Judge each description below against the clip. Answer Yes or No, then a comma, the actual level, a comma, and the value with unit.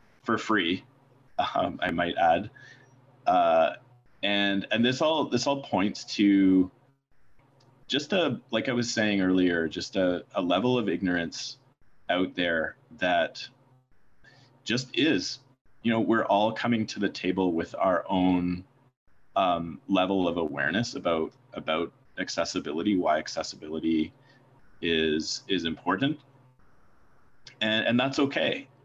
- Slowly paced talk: Yes, slow, 125 wpm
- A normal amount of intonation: No, wide, 6.4 semitones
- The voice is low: Yes, low, 115 Hz